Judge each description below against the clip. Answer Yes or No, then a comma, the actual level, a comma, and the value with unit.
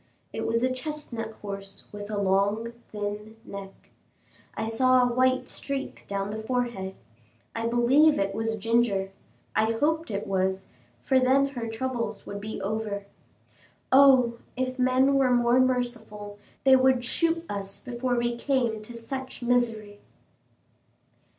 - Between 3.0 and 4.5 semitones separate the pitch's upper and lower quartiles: Yes, average, 3.7 semitones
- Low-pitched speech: No, high, 235 Hz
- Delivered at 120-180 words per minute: Yes, average, 140 wpm